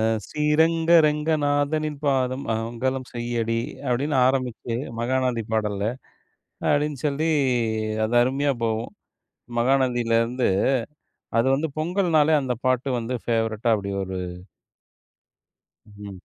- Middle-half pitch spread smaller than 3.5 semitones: No, average, 4.2 semitones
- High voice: No, low, 130 Hz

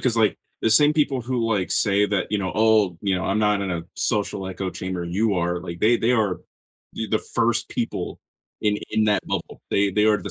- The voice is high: No, low, 105 Hz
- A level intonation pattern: No, average, 3.0 semitones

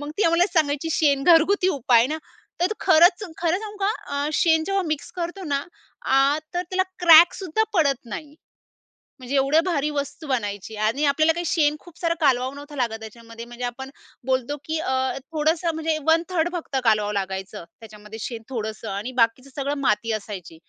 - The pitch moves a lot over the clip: Yes, wide, 5.7 semitones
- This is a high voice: Yes, very high, 285 Hz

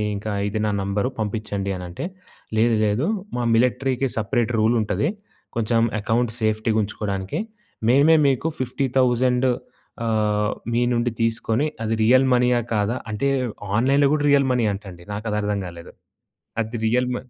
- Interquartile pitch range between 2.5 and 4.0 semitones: Yes, average, 3.1 semitones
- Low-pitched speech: Yes, low, 115 Hz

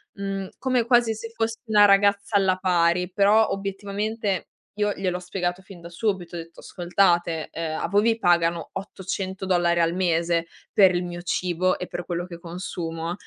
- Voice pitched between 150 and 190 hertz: Yes, medium, 185 Hz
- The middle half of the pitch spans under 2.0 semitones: No, narrow, 2.6 semitones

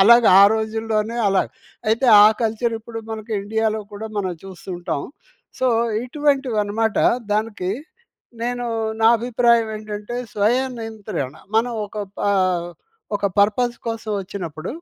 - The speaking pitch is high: Yes, high, 220 Hz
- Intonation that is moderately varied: No, narrow, 2.3 semitones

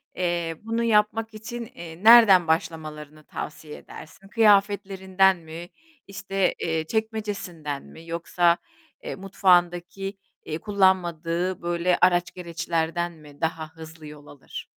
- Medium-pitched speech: Yes, medium, 175 Hz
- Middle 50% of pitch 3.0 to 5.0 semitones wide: Yes, average, 3.3 semitones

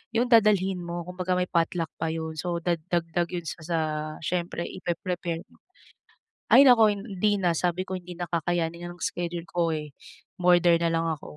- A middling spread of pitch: No, narrow, 1.5 semitones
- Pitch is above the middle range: No, medium, 175 Hz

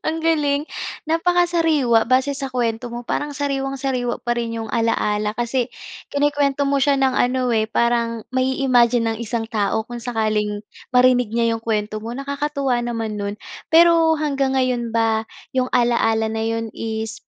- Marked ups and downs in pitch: No, average, 3.5 semitones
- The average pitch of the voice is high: Yes, high, 245 Hz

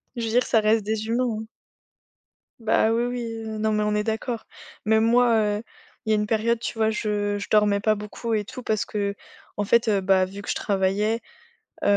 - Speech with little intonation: Yes, narrow, 1.6 semitones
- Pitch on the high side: Yes, high, 220 Hz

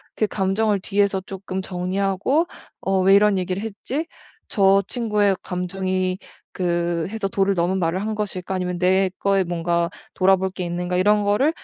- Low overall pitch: No, high, 190 Hz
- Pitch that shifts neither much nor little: No, narrow, 1.9 semitones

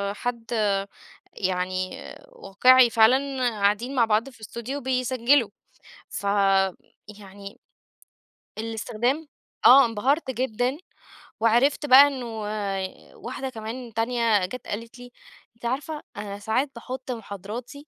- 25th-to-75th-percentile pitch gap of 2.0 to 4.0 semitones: Yes, average, 3.5 semitones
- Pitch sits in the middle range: No, high, 235 Hz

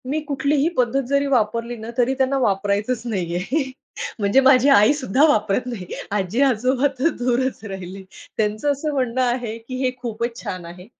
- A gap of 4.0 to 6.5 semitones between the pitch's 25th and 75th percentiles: Yes, average, 4.3 semitones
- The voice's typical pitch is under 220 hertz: No, high, 240 Hz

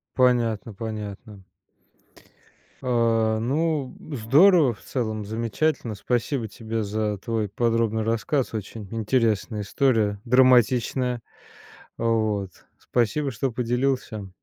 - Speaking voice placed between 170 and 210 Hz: No, low, 115 Hz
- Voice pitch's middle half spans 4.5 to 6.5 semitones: No, average, 2.7 semitones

